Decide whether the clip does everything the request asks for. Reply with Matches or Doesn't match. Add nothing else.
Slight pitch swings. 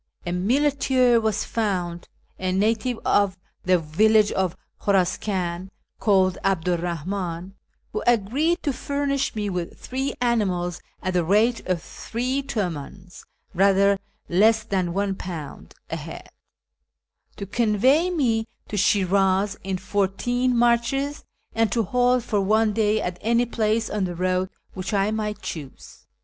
Doesn't match